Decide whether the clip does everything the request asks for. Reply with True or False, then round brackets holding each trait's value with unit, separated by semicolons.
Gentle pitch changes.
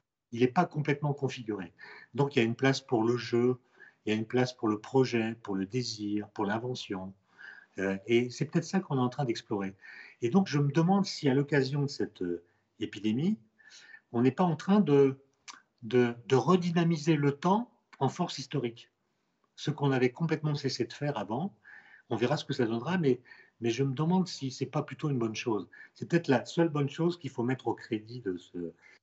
False (4.3 semitones)